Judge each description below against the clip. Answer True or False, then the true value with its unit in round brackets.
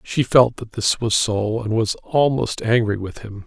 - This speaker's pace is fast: True (210 wpm)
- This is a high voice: False (110 Hz)